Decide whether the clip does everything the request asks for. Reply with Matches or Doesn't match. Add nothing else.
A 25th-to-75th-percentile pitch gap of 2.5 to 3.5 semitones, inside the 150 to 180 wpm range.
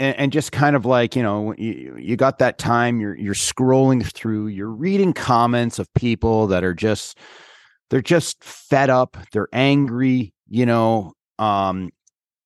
Doesn't match